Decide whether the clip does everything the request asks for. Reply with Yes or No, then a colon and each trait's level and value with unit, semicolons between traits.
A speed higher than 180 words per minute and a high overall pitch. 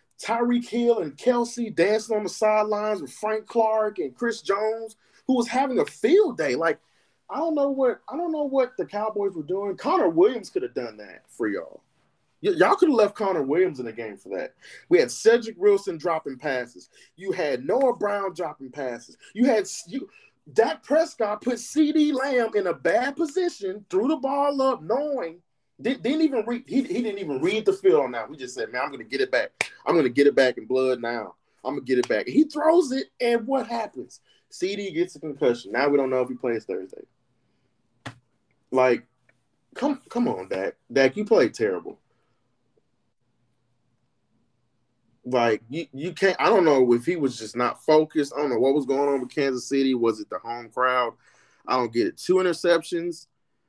Yes: average, 200 wpm; high, 205 Hz